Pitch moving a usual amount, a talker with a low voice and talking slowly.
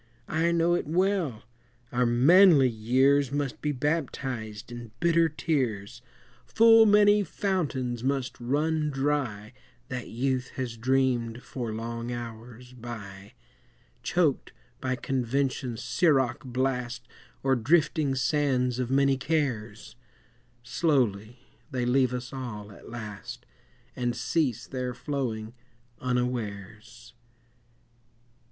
Yes: average, 3.3 semitones; low, 125 Hz; slow, 105 wpm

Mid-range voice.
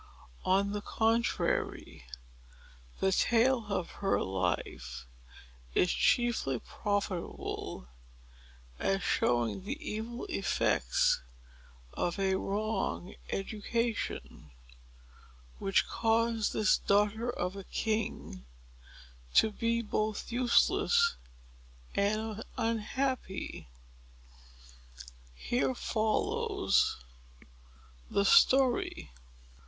No: high, 215 Hz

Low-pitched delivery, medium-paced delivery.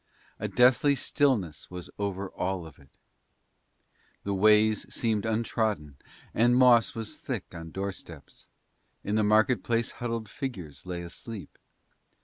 No: low, 105 Hz; slow, 130 wpm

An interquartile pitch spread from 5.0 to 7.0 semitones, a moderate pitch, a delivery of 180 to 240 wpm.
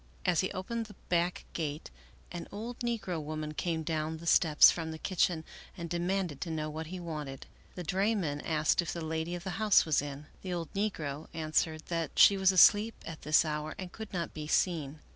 No: average, 3.2 semitones; medium, 165 Hz; fast, 205 wpm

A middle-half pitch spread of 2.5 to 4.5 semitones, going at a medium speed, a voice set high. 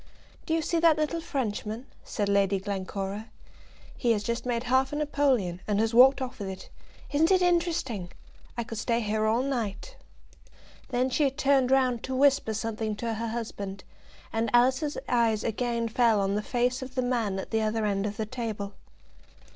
Yes: average, 3.8 semitones; average, 185 wpm; high, 235 Hz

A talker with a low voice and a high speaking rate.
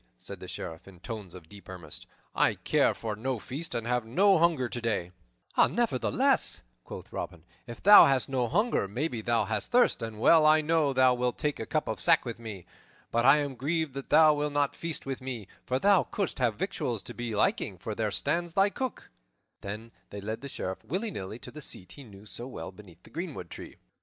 Yes: low, 125 Hz; fast, 210 wpm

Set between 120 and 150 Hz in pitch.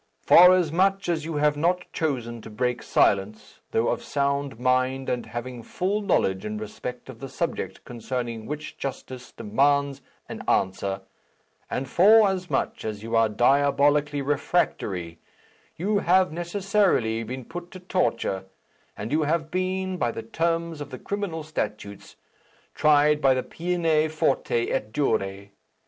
Yes: medium, 140 Hz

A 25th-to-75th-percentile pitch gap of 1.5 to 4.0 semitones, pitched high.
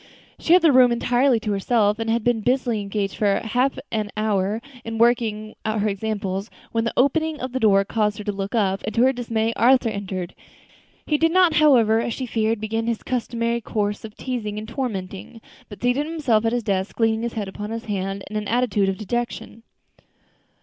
Yes: average, 2.8 semitones; high, 225 Hz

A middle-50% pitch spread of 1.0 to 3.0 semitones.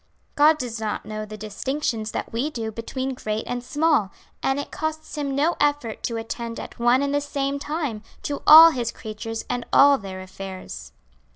No: average, 4.8 semitones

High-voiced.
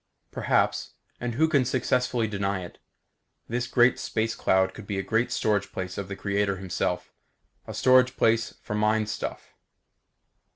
No: low, 110 Hz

